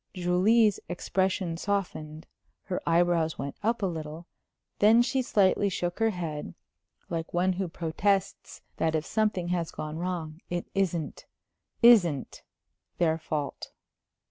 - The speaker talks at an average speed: No, slow, 125 wpm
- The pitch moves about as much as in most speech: Yes, average, 3.4 semitones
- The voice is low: No, medium, 175 Hz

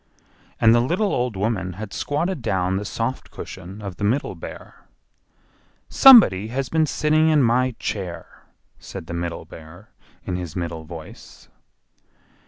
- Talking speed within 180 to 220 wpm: No, average, 145 wpm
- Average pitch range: No, wide, 6.7 semitones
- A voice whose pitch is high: No, low, 105 Hz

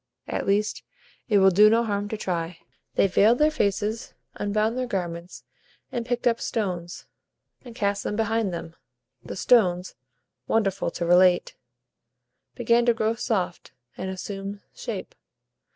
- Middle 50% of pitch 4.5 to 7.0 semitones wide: No, average, 3.6 semitones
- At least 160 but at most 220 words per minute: No, average, 140 wpm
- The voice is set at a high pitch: Yes, high, 205 Hz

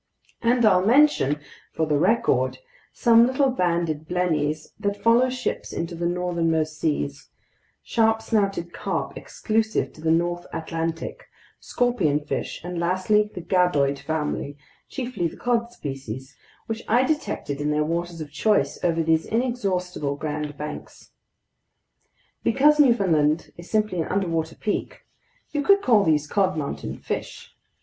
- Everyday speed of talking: No, slow, 130 wpm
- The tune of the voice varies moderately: No, wide, 6.4 semitones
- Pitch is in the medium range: Yes, medium, 175 Hz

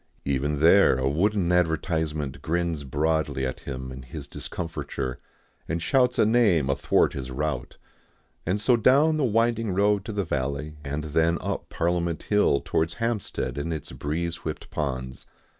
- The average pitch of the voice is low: Yes, very low, 80 Hz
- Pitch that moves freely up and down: Yes, wide, 6.2 semitones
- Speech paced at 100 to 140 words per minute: No, average, 155 wpm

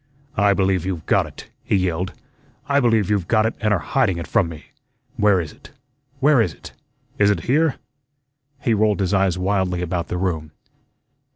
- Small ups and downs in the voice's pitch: No, average, 3.4 semitones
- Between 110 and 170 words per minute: No, average, 185 wpm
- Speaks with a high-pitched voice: No, very low, 95 Hz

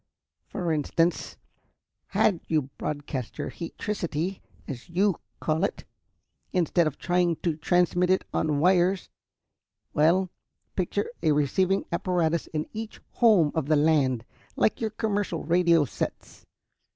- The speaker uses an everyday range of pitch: Yes, average, 3.4 semitones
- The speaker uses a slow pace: Yes, slow, 125 wpm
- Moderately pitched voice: Yes, medium, 170 Hz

